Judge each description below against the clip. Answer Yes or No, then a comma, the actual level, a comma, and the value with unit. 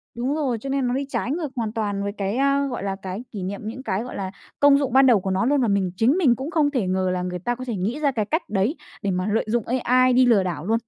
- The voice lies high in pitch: Yes, high, 235 Hz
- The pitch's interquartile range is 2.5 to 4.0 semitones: No, average, 5.2 semitones